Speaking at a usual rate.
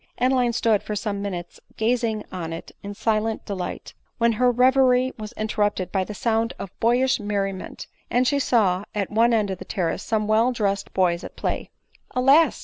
Yes: average, 180 wpm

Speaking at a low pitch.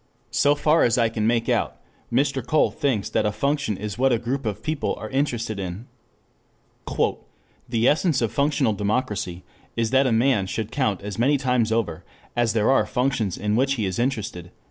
Yes: low, 115 Hz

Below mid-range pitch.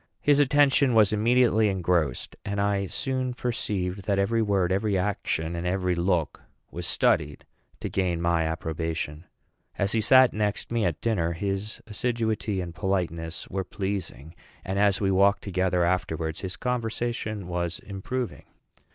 Yes: low, 100 Hz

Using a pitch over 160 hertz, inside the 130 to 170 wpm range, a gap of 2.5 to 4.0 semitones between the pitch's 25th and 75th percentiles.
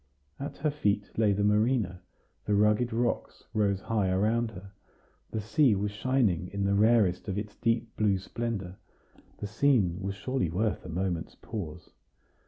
No: low, 105 Hz; average, 160 wpm; average, 3.0 semitones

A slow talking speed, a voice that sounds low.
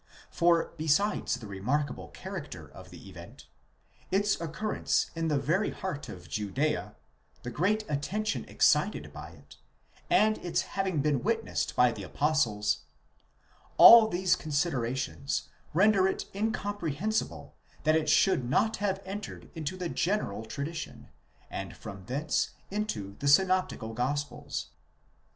No: slow, 125 wpm; medium, 160 Hz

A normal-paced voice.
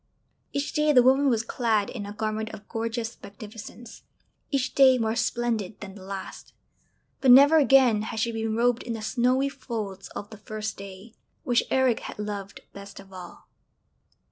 Yes: average, 170 wpm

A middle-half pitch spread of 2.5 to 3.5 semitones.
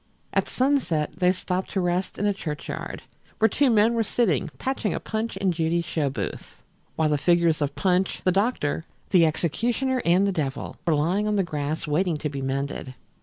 No: average, 5.2 semitones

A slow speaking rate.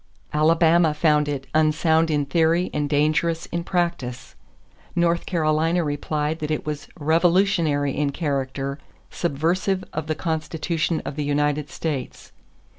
Yes: slow, 125 wpm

